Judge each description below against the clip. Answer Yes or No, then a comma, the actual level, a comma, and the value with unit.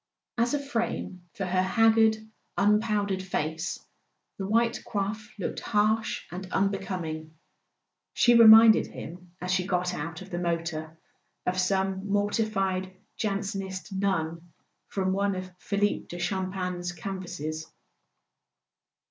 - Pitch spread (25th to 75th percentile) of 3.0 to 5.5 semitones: No, narrow, 2.6 semitones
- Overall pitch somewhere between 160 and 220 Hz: Yes, high, 190 Hz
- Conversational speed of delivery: No, slow, 120 wpm